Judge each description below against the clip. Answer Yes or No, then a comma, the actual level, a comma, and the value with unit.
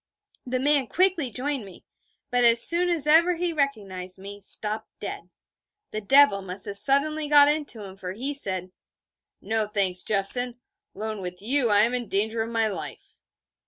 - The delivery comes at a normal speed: Yes, average, 170 wpm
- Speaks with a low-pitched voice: No, high, 230 Hz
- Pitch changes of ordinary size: No, wide, 6.2 semitones